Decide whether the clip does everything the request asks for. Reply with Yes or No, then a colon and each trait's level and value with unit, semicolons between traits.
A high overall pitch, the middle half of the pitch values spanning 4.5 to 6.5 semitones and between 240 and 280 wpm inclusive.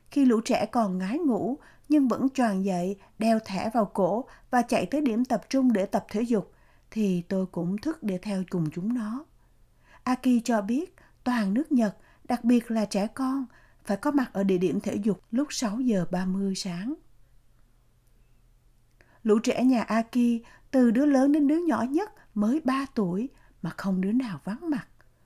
No: high, 225 Hz; average, 5.0 semitones; average, 185 wpm